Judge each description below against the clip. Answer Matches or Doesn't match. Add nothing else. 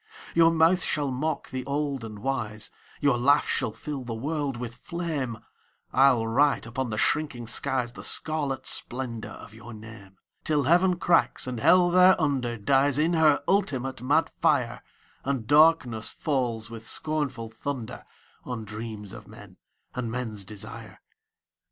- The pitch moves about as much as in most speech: Matches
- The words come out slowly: Doesn't match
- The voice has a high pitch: Doesn't match